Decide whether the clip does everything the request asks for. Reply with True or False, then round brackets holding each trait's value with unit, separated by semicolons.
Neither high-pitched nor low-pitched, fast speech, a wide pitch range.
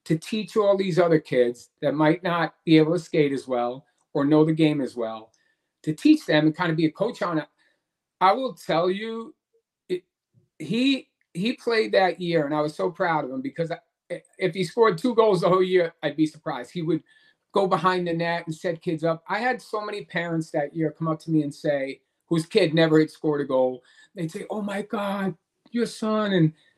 False (170 Hz; 225 wpm; 4.8 semitones)